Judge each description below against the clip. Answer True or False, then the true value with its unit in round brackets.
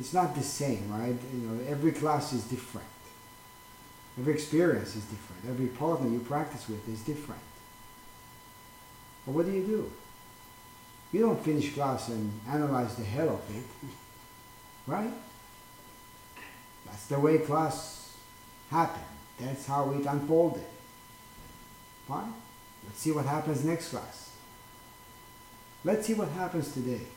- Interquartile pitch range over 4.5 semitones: True (5.0 semitones)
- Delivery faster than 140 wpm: False (135 wpm)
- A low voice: True (125 Hz)